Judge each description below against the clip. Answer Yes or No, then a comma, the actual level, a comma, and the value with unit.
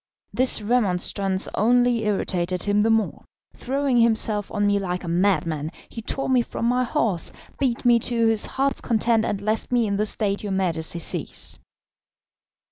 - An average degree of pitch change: Yes, average, 3.6 semitones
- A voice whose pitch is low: No, high, 215 Hz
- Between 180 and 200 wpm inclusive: No, average, 165 wpm